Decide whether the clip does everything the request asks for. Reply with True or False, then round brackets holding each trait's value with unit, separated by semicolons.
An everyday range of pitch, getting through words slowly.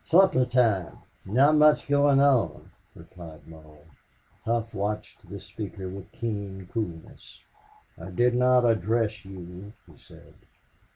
True (5.0 semitones; 120 wpm)